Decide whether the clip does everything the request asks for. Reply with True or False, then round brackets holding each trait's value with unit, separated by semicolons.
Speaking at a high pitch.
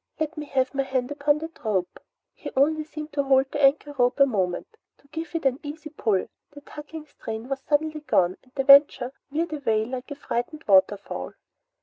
True (275 Hz)